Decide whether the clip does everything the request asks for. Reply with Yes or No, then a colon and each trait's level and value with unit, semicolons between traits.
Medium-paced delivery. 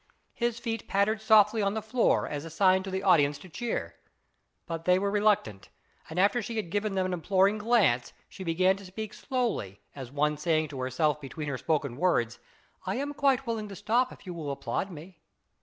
No: fast, 210 wpm